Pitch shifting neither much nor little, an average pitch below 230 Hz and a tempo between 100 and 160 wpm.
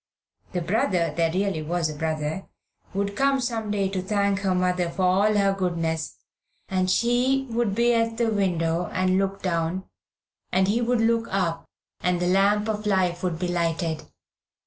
No: average, 3.3 semitones; high, 190 Hz; average, 170 wpm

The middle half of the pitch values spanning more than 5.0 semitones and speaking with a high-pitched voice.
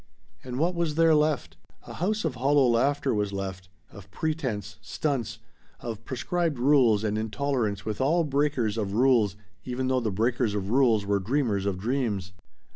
No: wide, 5.5 semitones; low, 120 Hz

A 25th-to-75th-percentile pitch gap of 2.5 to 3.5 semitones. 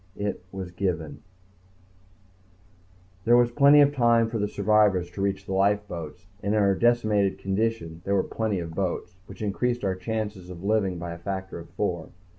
Yes: average, 3.2 semitones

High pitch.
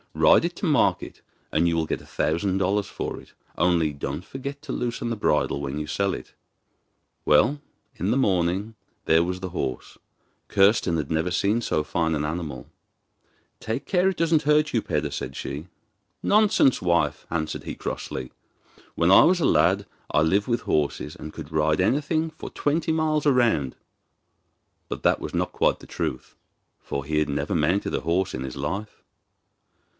No: very low, 90 Hz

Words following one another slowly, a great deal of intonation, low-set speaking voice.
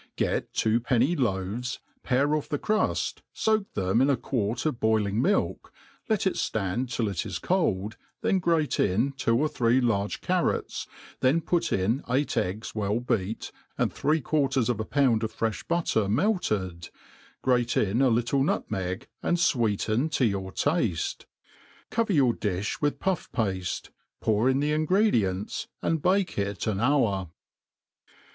No: average, 155 wpm; wide, 6.2 semitones; low, 120 Hz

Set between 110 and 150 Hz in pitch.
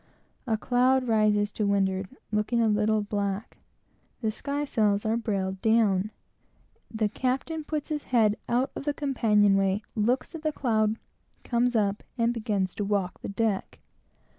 No: high, 220 Hz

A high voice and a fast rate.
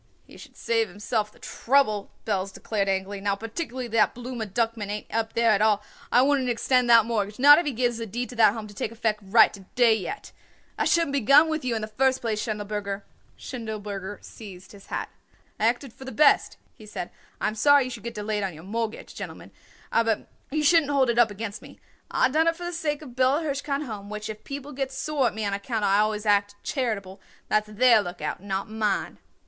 Yes: high, 225 Hz; fast, 220 wpm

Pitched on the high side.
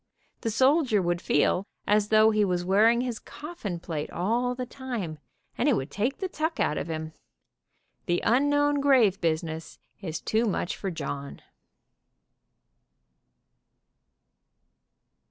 Yes: high, 215 Hz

